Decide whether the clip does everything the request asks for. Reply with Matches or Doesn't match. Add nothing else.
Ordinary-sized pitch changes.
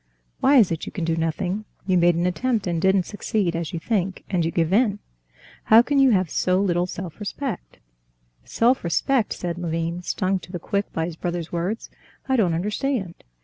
Matches